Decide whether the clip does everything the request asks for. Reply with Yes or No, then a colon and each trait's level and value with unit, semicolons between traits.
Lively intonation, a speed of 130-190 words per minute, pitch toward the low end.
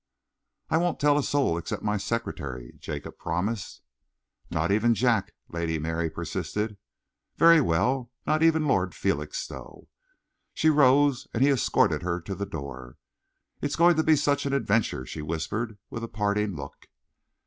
Yes: wide, 9.0 semitones; average, 150 wpm; low, 110 Hz